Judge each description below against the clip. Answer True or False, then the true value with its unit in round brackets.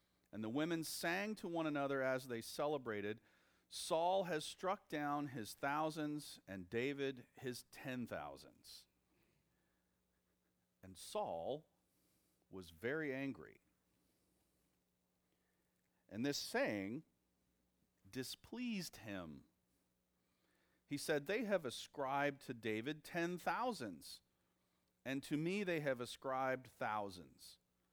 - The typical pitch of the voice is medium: False (120 Hz)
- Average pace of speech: False (100 wpm)